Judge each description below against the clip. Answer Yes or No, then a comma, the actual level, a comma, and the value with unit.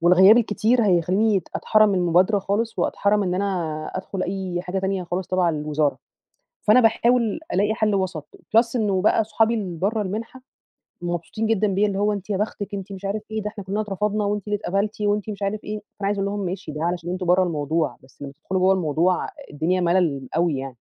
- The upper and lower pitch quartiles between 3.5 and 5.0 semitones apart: No, average, 3.1 semitones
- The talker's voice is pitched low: No, high, 195 Hz